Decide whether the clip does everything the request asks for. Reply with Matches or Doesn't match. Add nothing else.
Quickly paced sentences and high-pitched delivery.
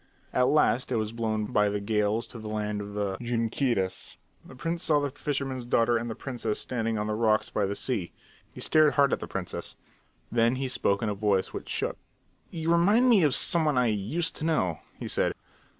Doesn't match